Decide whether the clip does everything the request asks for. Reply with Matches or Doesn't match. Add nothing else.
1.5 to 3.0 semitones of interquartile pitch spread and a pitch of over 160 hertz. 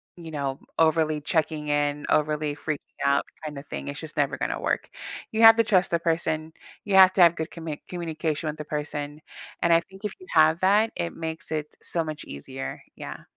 Doesn't match